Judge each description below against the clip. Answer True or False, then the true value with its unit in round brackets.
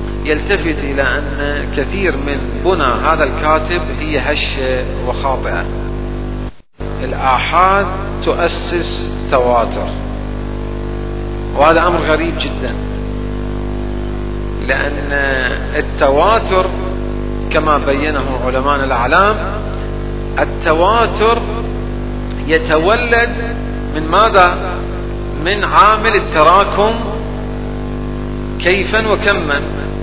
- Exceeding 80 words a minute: False (65 wpm)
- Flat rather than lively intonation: False (3.2 semitones)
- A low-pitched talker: True (125 Hz)